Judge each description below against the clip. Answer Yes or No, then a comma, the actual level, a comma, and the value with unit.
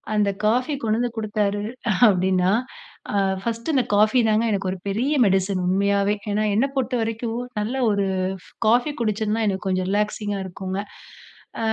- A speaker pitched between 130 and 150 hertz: No, high, 210 Hz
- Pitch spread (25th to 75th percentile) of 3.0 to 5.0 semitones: No, narrow, 2.6 semitones